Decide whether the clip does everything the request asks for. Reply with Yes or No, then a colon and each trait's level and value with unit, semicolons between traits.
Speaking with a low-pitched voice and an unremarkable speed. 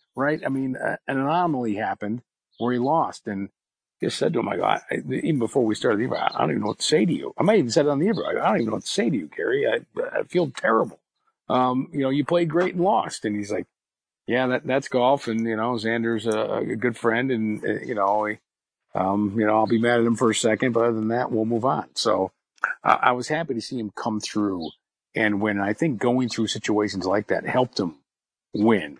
No: low, 115 Hz; fast, 255 wpm